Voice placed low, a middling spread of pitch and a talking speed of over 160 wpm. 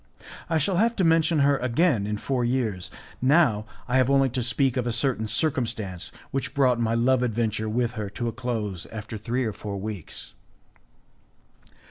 Yes: low, 120 Hz; average, 3.8 semitones; average, 175 wpm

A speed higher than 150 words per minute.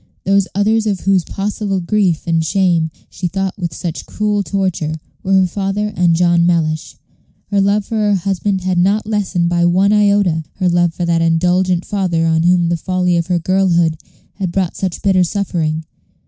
Yes: average, 180 wpm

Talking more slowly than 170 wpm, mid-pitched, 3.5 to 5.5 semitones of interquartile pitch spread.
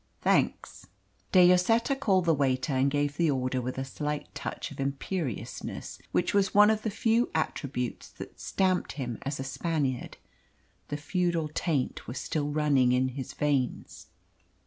Yes: average, 155 wpm; medium, 145 Hz; average, 5.2 semitones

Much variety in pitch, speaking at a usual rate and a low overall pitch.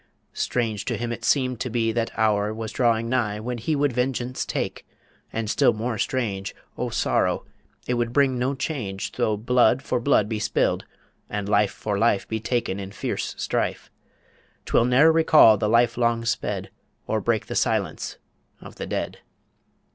No: narrow, 2.6 semitones; average, 170 wpm; low, 115 Hz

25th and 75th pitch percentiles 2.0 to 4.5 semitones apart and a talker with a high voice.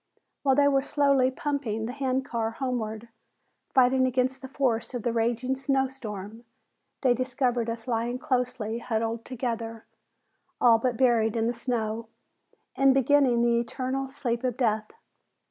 Yes: narrow, 2.5 semitones; high, 245 Hz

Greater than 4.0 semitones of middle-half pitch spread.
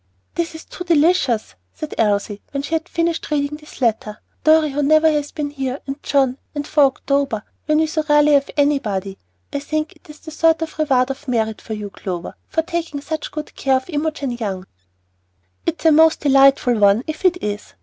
No: average, 3.7 semitones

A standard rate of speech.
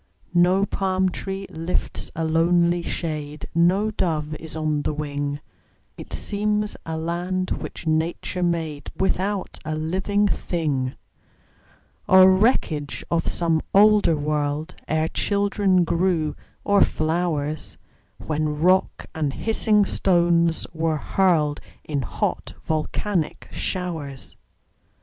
No: slow, 110 wpm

